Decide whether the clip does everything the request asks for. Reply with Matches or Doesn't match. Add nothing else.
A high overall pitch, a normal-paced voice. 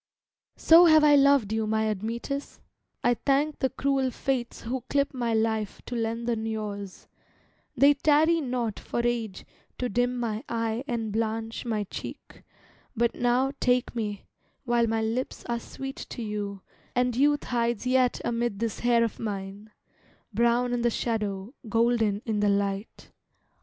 Matches